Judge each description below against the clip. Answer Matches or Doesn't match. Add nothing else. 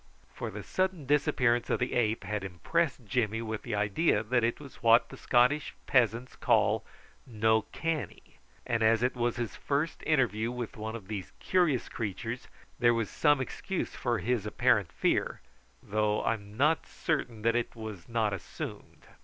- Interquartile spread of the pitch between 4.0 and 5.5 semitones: Doesn't match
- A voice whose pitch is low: Matches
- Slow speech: Doesn't match